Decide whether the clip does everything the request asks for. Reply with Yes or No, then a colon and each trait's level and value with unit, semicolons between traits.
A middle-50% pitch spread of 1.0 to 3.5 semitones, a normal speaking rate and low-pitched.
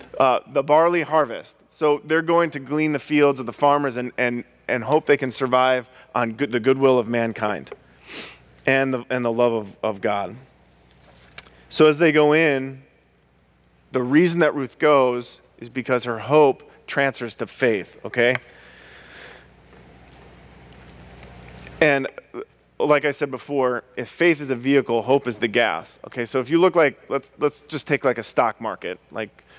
No: average, 4.0 semitones; average, 165 wpm; low, 130 Hz